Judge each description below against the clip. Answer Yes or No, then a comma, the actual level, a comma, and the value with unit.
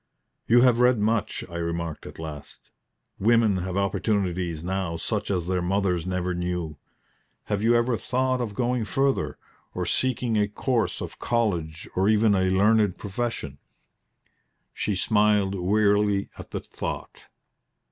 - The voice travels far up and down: No, average, 4.0 semitones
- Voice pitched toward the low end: Yes, low, 100 Hz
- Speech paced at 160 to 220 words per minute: No, average, 140 wpm